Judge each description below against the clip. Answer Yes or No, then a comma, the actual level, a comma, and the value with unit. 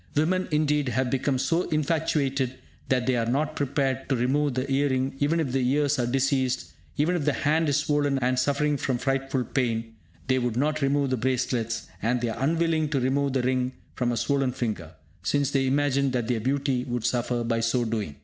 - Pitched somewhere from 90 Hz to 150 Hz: Yes, low, 135 Hz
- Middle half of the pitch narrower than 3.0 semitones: Yes, narrow, 2.6 semitones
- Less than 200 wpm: No, fast, 205 wpm